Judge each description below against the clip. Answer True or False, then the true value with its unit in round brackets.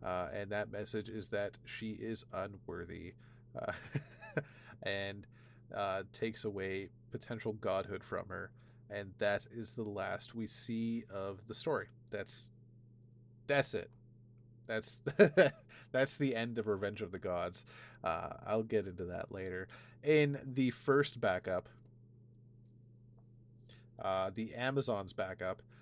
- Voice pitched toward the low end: True (115 Hz)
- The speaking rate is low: True (125 wpm)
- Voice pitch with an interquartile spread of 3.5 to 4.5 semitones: False (2.4 semitones)